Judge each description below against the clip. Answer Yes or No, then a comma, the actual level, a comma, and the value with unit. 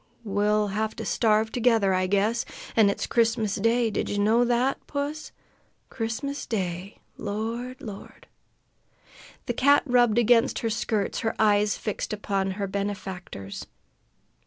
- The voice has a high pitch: Yes, high, 220 Hz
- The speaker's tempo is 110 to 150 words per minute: Yes, slow, 135 wpm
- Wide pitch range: No, average, 2.8 semitones